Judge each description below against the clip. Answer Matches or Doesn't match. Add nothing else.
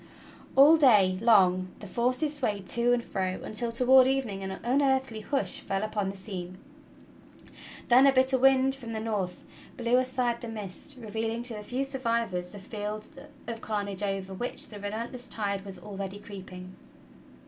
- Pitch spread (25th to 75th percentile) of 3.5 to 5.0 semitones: Matches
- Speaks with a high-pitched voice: Matches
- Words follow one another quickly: Doesn't match